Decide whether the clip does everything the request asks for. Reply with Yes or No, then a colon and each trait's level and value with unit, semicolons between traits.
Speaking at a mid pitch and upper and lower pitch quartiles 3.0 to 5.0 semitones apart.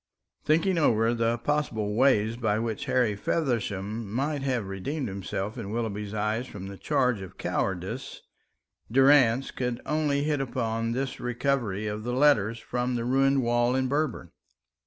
No: low, 120 Hz; average, 4.1 semitones